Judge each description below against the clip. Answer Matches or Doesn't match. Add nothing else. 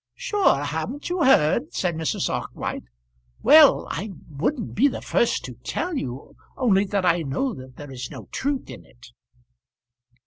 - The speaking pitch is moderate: Doesn't match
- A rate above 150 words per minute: Matches